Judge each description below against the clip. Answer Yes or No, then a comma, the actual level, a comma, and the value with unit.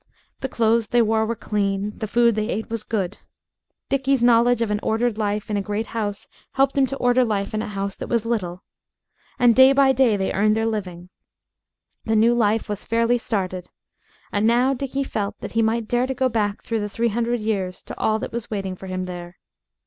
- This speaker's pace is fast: Yes, fast, 215 wpm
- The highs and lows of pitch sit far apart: No, average, 2.7 semitones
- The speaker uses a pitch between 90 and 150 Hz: No, high, 220 Hz